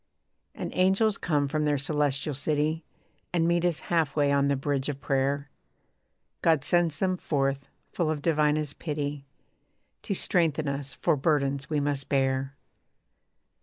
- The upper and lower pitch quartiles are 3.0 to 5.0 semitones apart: No, narrow, 2.6 semitones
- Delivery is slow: No, average, 145 wpm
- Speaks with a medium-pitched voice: Yes, medium, 145 Hz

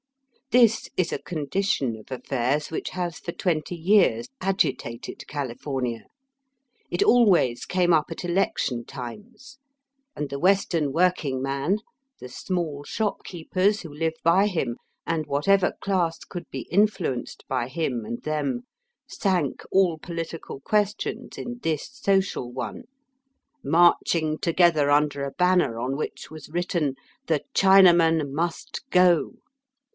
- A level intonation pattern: No, average, 5.1 semitones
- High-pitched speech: No, medium, 165 Hz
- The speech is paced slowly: Yes, slow, 130 wpm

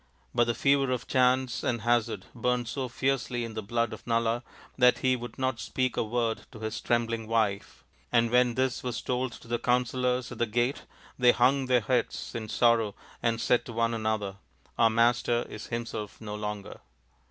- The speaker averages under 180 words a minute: No, average, 190 wpm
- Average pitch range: No, narrow, 1.7 semitones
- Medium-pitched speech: No, low, 120 Hz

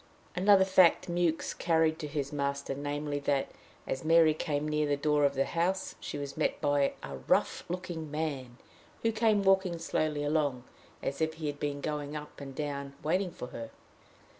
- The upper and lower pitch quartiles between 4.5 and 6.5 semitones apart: No, average, 2.8 semitones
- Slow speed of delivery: No, average, 180 wpm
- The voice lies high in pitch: No, medium, 150 Hz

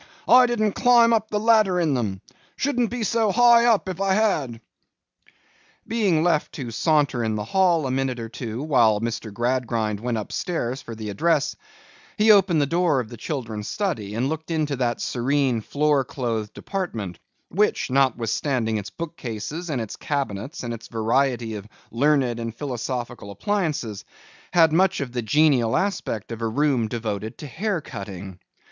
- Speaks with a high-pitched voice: No, low, 135 Hz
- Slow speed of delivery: No, average, 165 wpm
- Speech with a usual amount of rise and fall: No, wide, 7.4 semitones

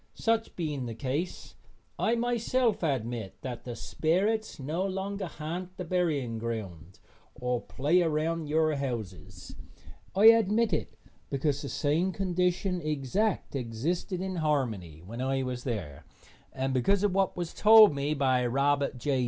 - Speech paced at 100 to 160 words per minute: Yes, average, 145 wpm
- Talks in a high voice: No, medium, 150 Hz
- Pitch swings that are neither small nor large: No, wide, 6.5 semitones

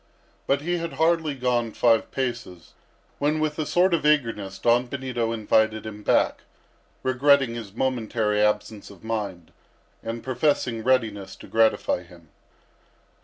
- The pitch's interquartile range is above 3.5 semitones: Yes, average, 4.4 semitones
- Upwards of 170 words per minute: No, slow, 135 wpm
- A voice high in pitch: No, low, 120 Hz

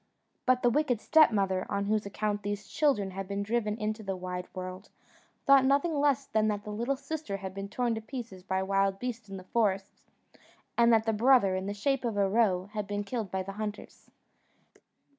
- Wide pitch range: No, average, 3.5 semitones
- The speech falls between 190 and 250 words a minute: Yes, average, 200 wpm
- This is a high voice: Yes, high, 210 Hz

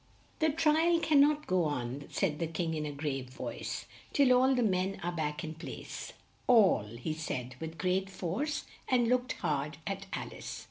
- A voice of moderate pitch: Yes, medium, 180 Hz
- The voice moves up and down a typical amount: No, wide, 8.9 semitones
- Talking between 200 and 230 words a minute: No, average, 190 wpm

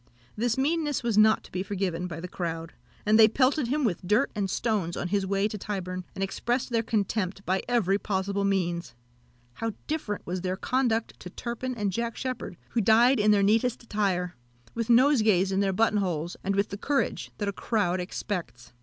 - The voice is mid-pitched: No, high, 205 Hz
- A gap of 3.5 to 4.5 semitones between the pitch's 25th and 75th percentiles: Yes, average, 3.9 semitones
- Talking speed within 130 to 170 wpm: No, average, 195 wpm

